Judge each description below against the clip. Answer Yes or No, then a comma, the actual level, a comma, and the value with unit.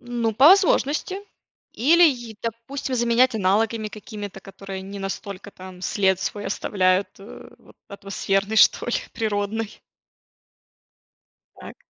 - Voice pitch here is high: Yes, high, 215 Hz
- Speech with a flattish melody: No, average, 3.3 semitones